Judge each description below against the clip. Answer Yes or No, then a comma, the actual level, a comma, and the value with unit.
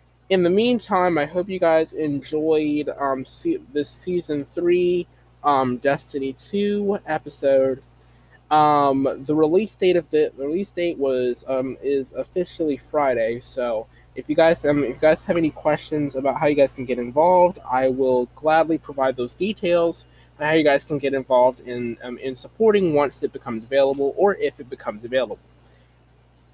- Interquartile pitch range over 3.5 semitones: Yes, average, 4.5 semitones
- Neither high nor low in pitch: Yes, medium, 145 Hz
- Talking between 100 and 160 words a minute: No, average, 170 wpm